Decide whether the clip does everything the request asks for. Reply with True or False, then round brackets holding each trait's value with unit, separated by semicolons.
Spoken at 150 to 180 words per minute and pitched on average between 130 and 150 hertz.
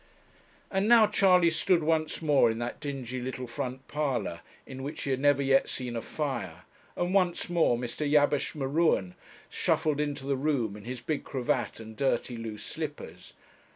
True (170 wpm; 140 Hz)